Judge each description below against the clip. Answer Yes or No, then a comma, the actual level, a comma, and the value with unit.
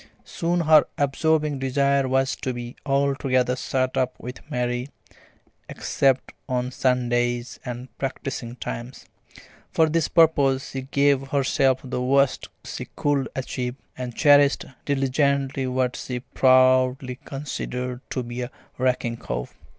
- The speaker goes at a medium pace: No, slow, 130 wpm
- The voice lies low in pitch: Yes, low, 130 Hz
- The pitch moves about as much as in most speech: No, narrow, 1.7 semitones